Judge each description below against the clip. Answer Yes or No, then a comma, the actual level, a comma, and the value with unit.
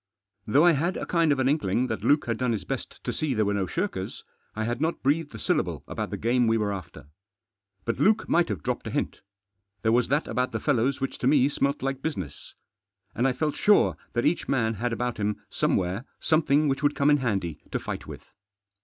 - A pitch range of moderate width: Yes, average, 4.8 semitones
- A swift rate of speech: Yes, fast, 225 wpm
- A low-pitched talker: Yes, low, 130 Hz